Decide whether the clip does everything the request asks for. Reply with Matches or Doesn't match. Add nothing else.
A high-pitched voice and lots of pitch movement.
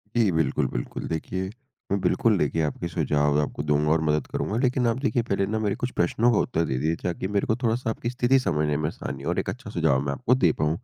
Doesn't match